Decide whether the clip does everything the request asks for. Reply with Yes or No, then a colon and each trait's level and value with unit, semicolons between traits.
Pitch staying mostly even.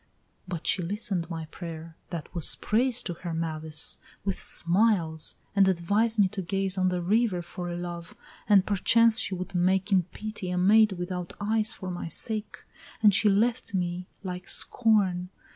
No: average, 3.2 semitones